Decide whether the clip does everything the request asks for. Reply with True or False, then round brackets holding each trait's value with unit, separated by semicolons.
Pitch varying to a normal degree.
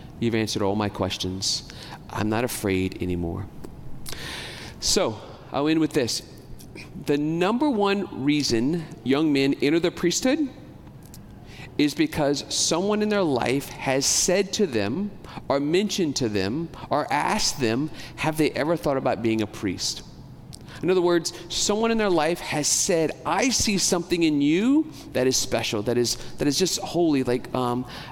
False (6.3 semitones)